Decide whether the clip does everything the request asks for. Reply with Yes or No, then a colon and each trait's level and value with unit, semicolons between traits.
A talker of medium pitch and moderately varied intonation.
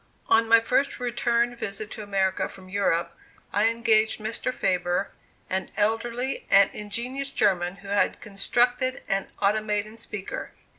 No: high, 215 Hz; average, 3.1 semitones